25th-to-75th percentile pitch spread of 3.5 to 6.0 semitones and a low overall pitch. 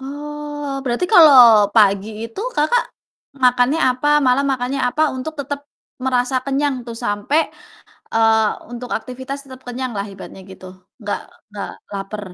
No: average, 4.1 semitones; very high, 255 Hz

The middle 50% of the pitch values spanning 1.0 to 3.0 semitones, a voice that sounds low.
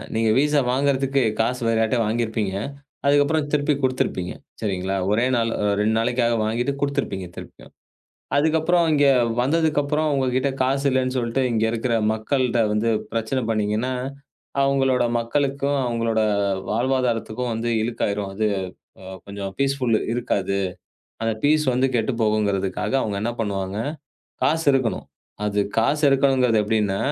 No: average, 4.0 semitones; low, 120 Hz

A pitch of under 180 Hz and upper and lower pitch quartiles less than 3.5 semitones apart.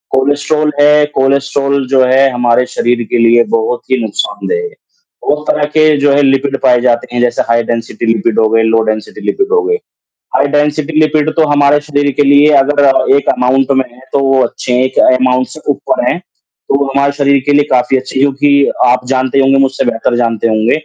Yes: low, 135 Hz; average, 2.8 semitones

